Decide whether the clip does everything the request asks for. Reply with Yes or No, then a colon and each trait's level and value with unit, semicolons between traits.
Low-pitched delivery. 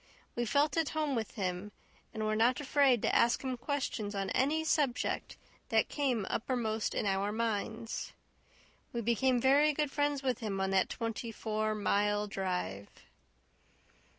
No: high, 230 Hz